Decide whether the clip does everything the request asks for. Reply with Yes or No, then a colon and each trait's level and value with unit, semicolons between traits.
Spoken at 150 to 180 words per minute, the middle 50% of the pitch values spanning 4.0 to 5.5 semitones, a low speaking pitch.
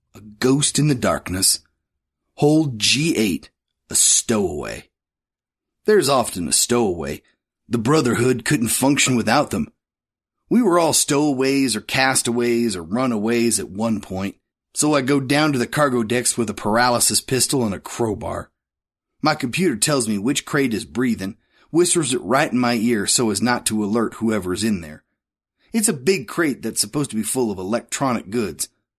Yes: average, 165 wpm; average, 4.9 semitones; low, 120 Hz